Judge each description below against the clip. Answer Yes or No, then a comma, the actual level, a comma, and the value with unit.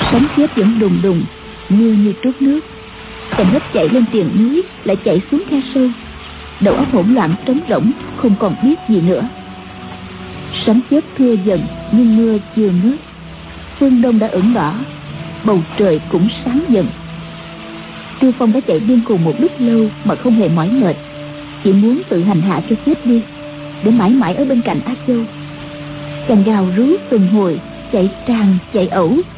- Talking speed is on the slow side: No, average, 180 wpm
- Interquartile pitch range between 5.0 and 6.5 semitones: Yes, average, 5.3 semitones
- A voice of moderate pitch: No, high, 220 Hz